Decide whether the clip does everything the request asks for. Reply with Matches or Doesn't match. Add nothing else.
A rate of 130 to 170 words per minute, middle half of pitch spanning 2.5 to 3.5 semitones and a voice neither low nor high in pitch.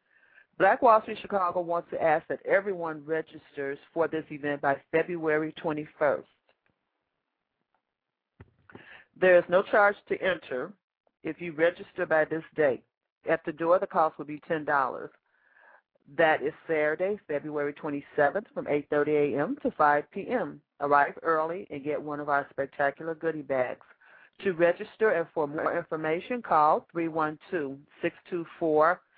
Matches